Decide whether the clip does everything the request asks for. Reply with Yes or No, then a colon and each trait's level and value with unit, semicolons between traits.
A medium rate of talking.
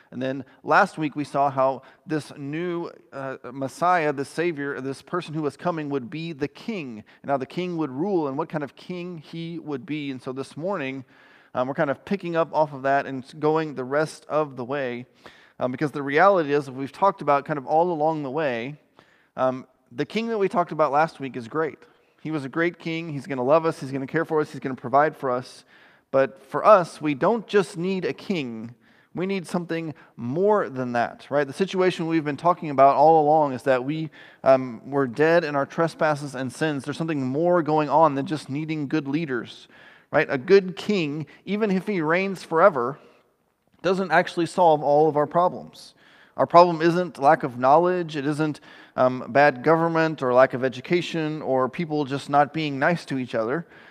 No: fast, 210 wpm